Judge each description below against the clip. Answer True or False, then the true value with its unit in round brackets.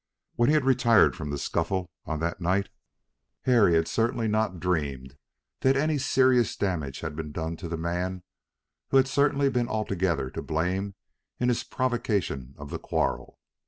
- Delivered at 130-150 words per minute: False (165 wpm)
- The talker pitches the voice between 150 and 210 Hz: False (95 Hz)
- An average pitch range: False (7.0 semitones)